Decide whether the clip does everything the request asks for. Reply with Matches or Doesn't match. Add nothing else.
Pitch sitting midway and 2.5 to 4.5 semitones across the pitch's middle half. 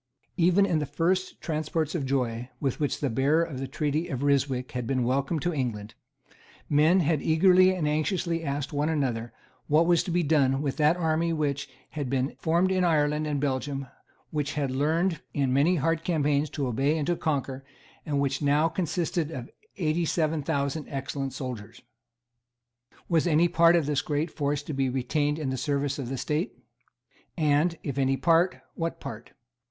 Matches